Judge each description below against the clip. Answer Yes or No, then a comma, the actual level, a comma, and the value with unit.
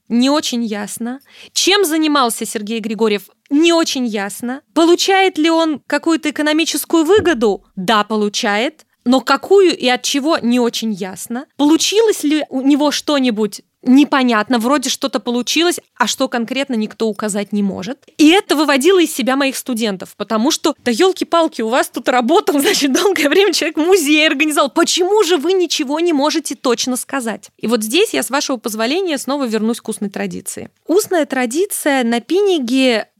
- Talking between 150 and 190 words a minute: Yes, fast, 160 wpm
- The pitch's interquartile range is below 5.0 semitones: No, wide, 5.5 semitones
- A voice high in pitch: Yes, very high, 275 Hz